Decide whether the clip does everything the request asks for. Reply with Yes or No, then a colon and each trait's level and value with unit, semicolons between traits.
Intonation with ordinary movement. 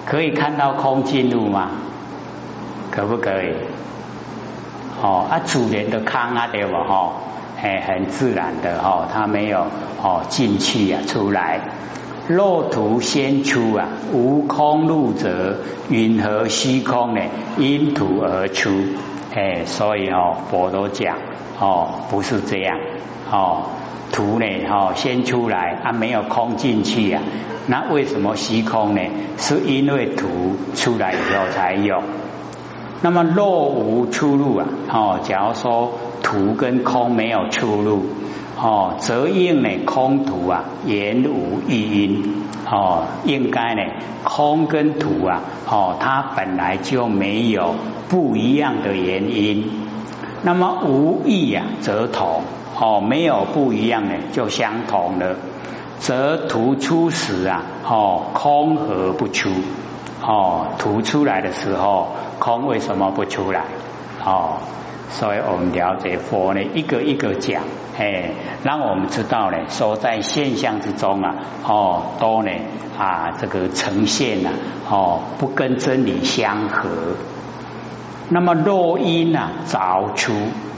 No: wide, 5.8 semitones